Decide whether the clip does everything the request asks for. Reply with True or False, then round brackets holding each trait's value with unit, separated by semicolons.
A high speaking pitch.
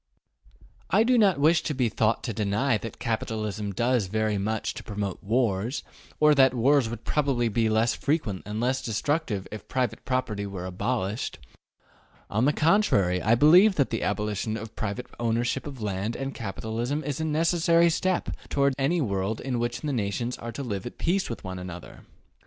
False (120 Hz)